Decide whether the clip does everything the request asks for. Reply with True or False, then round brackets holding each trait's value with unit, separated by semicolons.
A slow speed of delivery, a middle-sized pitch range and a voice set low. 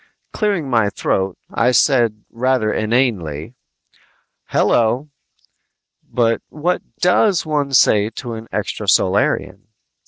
True (95 wpm; 4.6 semitones; 120 Hz)